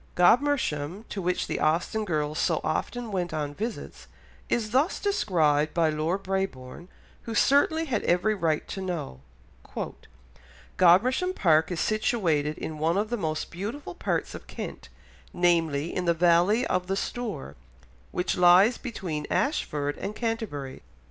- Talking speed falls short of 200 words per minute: Yes, average, 140 wpm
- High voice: No, medium, 180 Hz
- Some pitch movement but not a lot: No, wide, 5.7 semitones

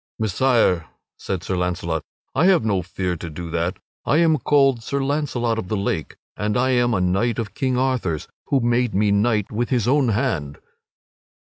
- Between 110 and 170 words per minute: No, average, 180 wpm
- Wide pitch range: Yes, wide, 5.9 semitones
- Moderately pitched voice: No, low, 115 Hz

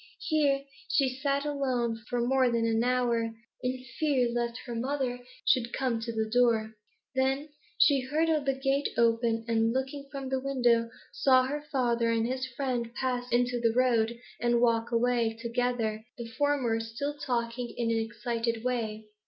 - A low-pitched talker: No, high, 245 Hz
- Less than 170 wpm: Yes, average, 160 wpm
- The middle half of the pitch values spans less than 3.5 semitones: Yes, narrow, 2.4 semitones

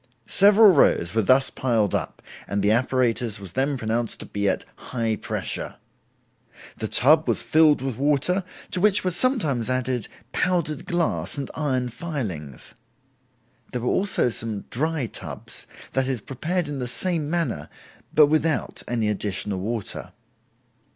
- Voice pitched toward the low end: Yes, low, 130 Hz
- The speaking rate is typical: Yes, average, 145 wpm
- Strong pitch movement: Yes, wide, 5.8 semitones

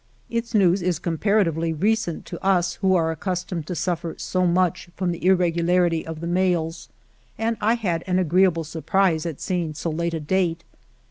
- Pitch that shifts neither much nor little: No, narrow, 2.3 semitones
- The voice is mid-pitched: Yes, medium, 175 Hz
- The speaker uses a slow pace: No, average, 175 wpm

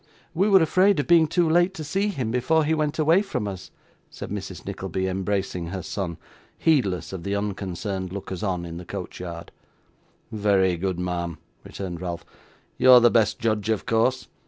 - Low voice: Yes, low, 105 Hz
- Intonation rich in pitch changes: Yes, wide, 8.7 semitones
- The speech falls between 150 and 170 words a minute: No, average, 180 wpm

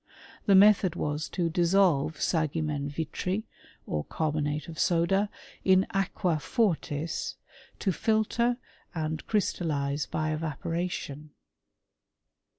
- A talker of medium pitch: Yes, medium, 165 Hz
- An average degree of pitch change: Yes, average, 3.9 semitones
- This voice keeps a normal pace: No, slow, 95 wpm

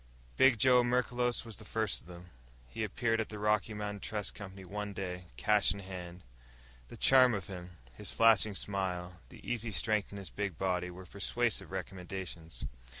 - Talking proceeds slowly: No, average, 175 wpm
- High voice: No, low, 100 Hz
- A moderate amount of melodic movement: Yes, average, 3.5 semitones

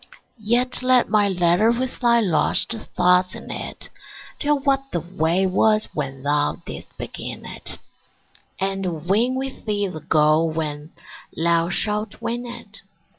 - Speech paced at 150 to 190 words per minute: No, average, 140 wpm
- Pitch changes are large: Yes, wide, 6.3 semitones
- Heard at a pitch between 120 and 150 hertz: No, high, 190 Hz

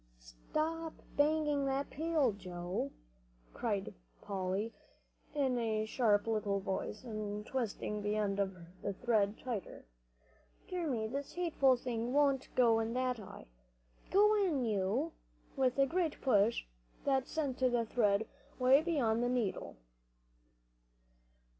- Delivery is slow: Yes, slow, 120 wpm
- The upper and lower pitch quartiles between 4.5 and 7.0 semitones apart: Yes, average, 5.0 semitones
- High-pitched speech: Yes, high, 240 Hz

